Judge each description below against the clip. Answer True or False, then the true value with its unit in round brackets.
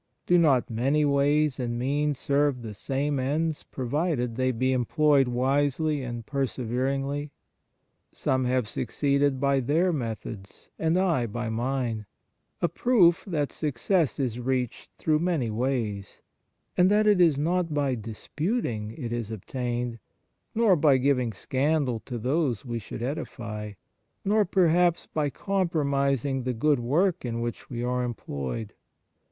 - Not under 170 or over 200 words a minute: False (135 wpm)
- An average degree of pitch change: True (4.2 semitones)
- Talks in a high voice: False (135 Hz)